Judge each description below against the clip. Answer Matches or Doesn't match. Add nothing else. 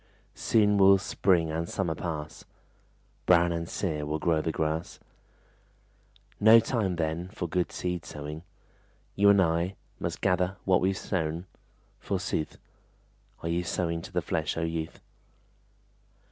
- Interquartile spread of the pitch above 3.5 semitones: Doesn't match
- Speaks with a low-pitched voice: Matches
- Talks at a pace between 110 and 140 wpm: Matches